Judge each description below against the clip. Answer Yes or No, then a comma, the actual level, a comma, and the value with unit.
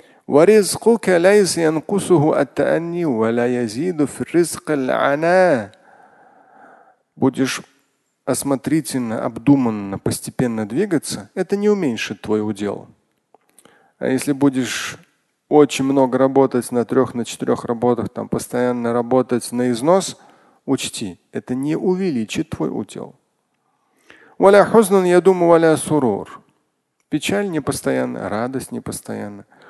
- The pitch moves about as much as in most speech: No, wide, 6.1 semitones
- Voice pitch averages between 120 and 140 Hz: Yes, low, 135 Hz